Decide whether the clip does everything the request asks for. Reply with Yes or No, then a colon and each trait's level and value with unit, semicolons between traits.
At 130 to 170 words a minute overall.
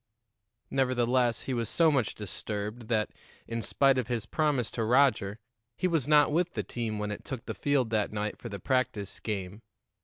No: average, 185 wpm